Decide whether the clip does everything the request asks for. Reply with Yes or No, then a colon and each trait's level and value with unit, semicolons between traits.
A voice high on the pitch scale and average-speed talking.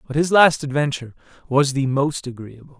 No: medium, 140 Hz; average, 170 wpm